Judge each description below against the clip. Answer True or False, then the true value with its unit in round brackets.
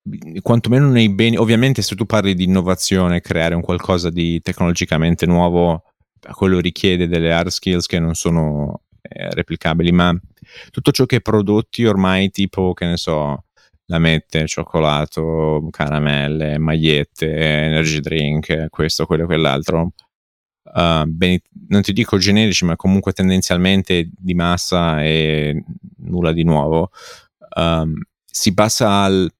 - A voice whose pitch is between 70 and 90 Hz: True (85 Hz)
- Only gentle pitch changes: False (3.1 semitones)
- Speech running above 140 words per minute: False (135 wpm)